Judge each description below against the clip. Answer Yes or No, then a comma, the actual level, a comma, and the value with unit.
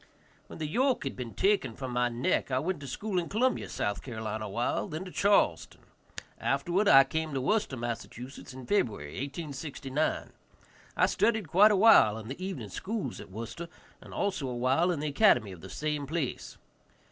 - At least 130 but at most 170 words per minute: No, average, 180 wpm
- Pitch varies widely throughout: Yes, wide, 7.3 semitones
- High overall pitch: No, medium, 140 Hz